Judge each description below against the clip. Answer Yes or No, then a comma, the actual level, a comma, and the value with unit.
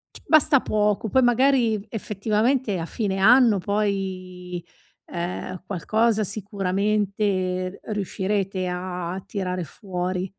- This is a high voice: Yes, high, 200 Hz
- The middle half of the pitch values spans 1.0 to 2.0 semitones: No, average, 2.7 semitones